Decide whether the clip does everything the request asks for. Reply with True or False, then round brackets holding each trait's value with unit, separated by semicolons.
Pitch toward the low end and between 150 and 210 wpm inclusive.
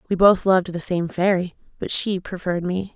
False (185 Hz; 205 wpm)